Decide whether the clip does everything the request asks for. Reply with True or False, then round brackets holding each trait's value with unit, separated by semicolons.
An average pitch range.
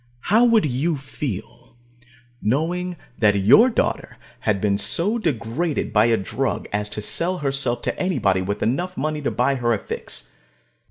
False (8.3 semitones)